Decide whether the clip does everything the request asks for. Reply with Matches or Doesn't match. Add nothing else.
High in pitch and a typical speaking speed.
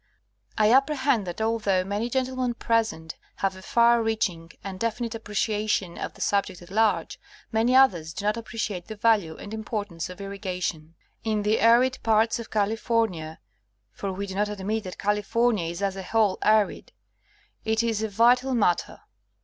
Matches